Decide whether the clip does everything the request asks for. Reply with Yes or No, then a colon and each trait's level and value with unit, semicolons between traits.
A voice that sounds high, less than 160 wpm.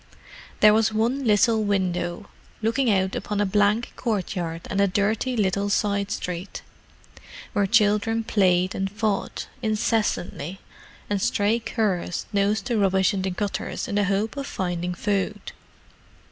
Yes: high, 205 Hz; average, 140 wpm